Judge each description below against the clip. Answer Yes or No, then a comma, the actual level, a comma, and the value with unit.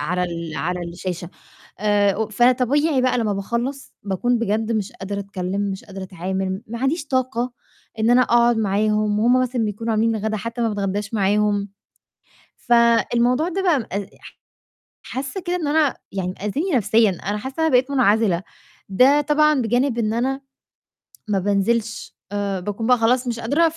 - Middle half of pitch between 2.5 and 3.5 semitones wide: No, average, 4.1 semitones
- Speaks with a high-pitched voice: Yes, high, 225 Hz